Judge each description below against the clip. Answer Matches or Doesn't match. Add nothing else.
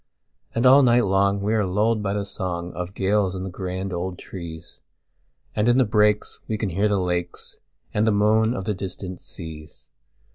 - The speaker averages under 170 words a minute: Doesn't match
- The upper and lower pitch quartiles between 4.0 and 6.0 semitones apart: Doesn't match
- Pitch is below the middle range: Matches